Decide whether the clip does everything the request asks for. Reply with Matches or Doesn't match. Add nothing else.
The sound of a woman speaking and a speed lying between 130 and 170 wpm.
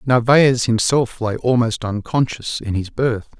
Doesn't match